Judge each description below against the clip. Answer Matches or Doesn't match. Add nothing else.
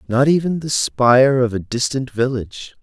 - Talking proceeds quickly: Doesn't match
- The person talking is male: Matches